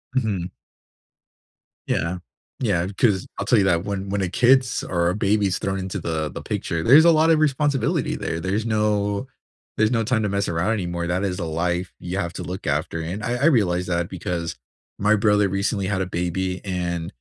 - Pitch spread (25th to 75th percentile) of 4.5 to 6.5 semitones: No, average, 3.6 semitones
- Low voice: Yes, very low, 95 Hz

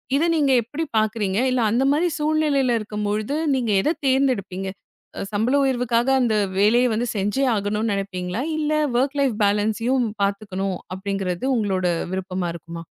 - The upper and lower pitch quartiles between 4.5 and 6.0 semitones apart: Yes, average, 4.9 semitones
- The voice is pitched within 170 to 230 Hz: Yes, high, 220 Hz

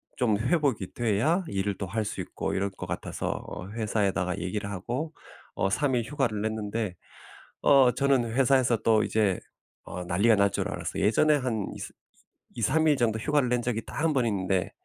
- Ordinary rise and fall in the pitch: Yes, average, 4.4 semitones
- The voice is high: No, low, 110 Hz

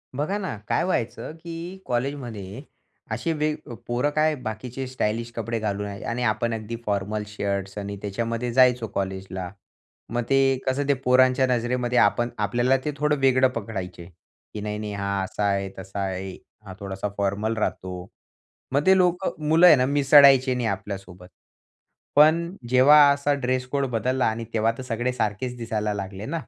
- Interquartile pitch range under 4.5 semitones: No, average, 4.8 semitones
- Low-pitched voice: Yes, low, 120 Hz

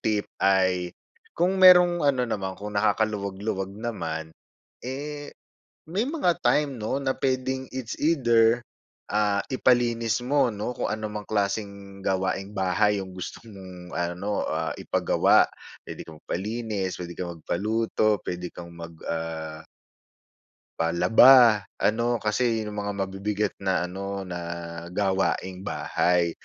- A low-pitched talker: Yes, low, 105 Hz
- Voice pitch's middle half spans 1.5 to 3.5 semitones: No, average, 4.2 semitones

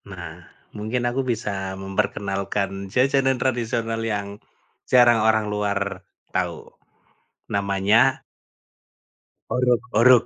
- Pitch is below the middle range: Yes, low, 110 Hz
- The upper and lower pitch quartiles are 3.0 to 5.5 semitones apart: Yes, average, 3.6 semitones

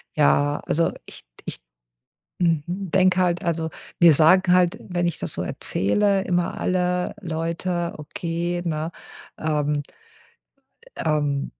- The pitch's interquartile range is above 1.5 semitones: Yes, narrow, 2.6 semitones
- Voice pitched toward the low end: No, medium, 170 Hz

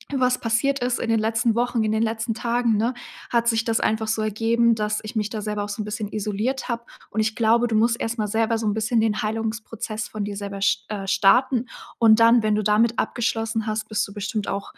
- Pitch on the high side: Yes, high, 220 Hz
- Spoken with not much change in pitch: Yes, narrow, 1.5 semitones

